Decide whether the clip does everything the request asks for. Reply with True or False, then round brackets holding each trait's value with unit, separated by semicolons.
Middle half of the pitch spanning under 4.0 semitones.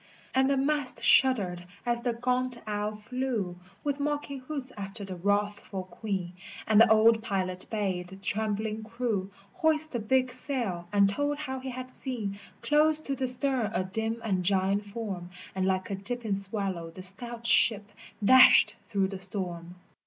False (4.8 semitones)